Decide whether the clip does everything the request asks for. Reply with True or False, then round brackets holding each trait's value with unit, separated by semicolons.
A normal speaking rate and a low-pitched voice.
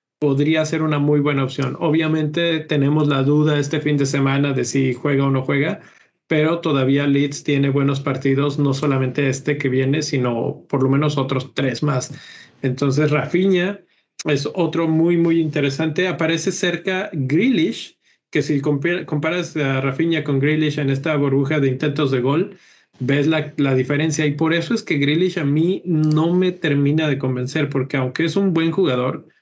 False (175 wpm; 150 Hz)